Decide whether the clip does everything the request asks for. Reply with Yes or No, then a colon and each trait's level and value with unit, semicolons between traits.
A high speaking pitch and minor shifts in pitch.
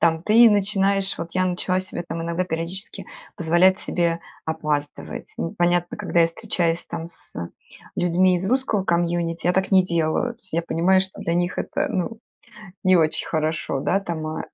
No: medium, 175 Hz; narrow, 2.2 semitones